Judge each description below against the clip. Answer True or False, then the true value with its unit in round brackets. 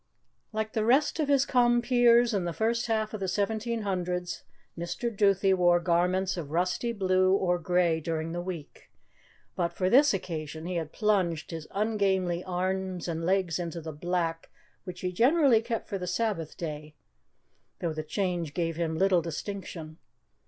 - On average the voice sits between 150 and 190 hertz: True (185 Hz)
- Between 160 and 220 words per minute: True (165 wpm)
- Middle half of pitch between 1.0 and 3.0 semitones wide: False (4.1 semitones)